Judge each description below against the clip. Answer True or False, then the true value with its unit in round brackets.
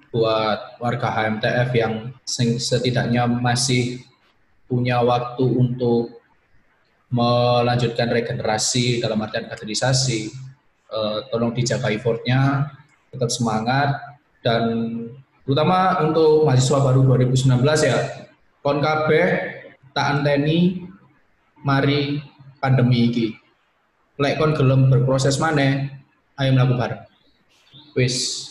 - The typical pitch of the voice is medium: False (125 Hz)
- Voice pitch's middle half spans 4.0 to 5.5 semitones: False (3.0 semitones)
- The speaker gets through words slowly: True (80 wpm)